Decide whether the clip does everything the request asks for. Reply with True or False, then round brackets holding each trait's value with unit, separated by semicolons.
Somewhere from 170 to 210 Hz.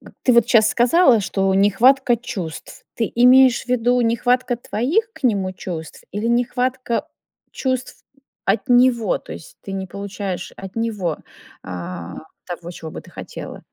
False (230 Hz)